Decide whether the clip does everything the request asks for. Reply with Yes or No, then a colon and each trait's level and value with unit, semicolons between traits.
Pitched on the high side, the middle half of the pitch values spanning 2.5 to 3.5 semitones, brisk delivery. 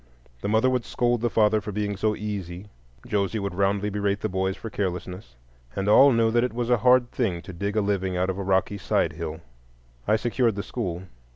No: low, 105 Hz; average, 2.9 semitones; fast, 215 wpm